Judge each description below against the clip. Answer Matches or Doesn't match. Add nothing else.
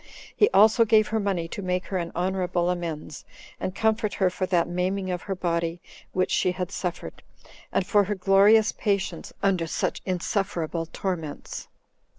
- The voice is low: Doesn't match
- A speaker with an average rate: Matches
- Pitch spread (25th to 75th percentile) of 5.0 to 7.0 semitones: Doesn't match